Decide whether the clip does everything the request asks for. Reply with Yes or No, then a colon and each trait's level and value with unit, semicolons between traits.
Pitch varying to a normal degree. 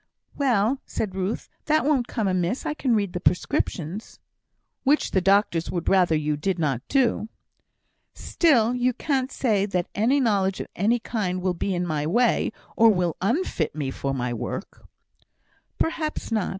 No: wide, 5.7 semitones